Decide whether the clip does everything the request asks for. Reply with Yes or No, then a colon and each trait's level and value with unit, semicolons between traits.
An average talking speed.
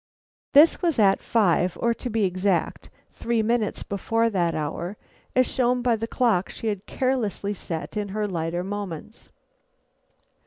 Yes: average, 150 wpm